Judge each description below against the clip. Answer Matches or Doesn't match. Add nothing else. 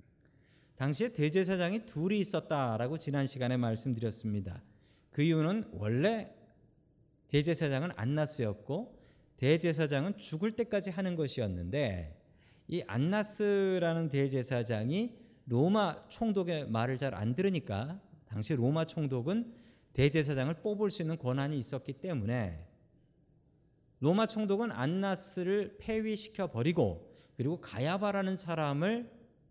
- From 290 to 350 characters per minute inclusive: Doesn't match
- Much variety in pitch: Matches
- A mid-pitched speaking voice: Matches